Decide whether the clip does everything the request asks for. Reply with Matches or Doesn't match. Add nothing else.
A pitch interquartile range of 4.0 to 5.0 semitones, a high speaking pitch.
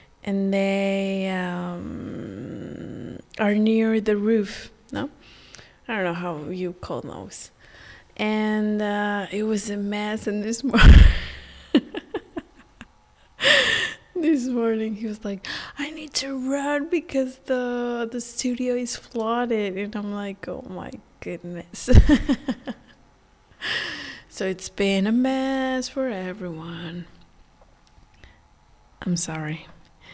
Doesn't match